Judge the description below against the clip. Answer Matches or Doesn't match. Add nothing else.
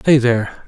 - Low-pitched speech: Matches